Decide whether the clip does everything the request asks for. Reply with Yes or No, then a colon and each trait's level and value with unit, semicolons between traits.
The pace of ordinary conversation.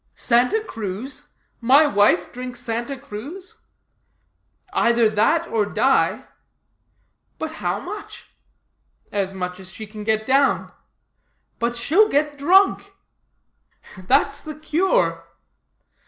No: slow, 105 wpm